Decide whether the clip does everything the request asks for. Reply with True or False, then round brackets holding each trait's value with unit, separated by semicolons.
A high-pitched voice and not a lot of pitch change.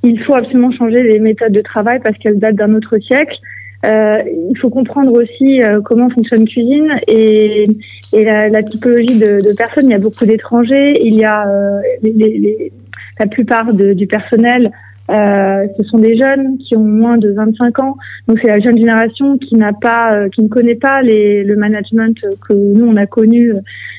True (220 Hz; 2.3 semitones)